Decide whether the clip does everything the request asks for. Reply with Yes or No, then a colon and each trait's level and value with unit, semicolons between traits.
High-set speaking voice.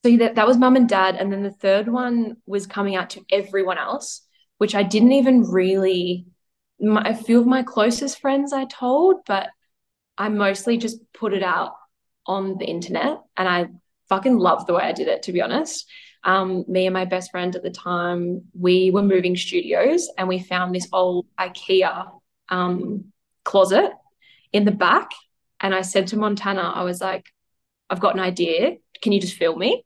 Yes: high, 195 Hz